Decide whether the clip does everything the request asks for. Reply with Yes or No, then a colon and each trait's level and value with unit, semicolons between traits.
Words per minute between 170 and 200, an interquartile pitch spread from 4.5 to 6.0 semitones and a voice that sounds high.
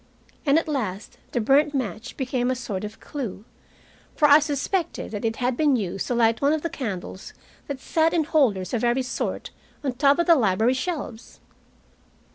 Yes: average, 190 wpm; average, 4.8 semitones; very high, 255 Hz